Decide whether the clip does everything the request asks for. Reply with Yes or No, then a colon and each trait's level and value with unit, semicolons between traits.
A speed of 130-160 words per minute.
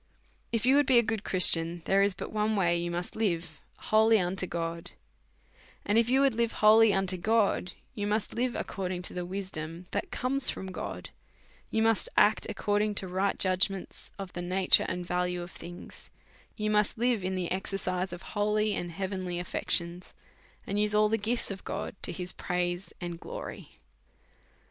No: average, 170 wpm